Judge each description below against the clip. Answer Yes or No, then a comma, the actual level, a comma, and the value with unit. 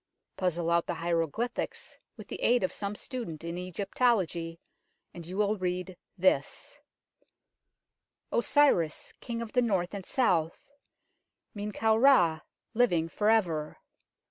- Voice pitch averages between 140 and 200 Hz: Yes, medium, 185 Hz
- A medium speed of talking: No, slow, 130 wpm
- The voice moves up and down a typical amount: Yes, average, 4.8 semitones